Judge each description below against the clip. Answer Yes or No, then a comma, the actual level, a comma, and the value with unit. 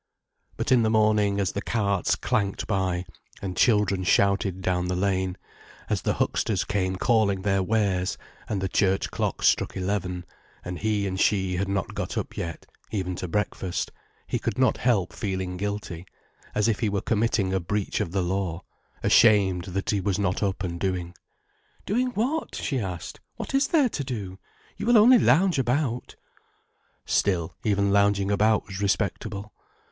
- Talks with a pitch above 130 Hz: No, low, 100 Hz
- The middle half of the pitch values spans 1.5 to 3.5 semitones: Yes, narrow, 2.6 semitones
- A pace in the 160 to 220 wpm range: Yes, average, 165 wpm